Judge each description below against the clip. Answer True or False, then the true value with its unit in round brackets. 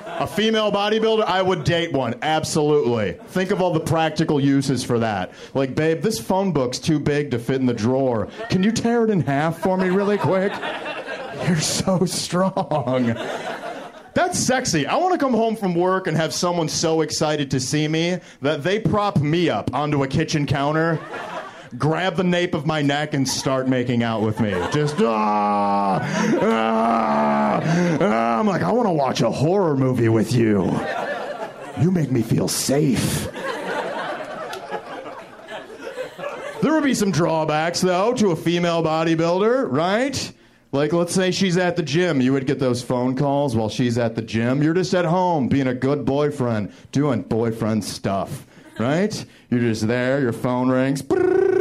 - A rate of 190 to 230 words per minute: False (170 wpm)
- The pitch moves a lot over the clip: True (6.3 semitones)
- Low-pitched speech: False (155 Hz)